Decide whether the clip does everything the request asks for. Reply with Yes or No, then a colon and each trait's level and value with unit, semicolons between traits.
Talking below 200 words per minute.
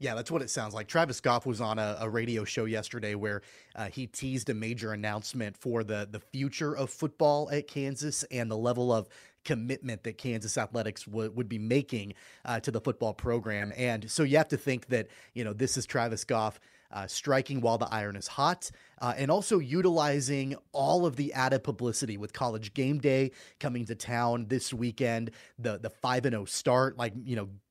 No: fast, 205 wpm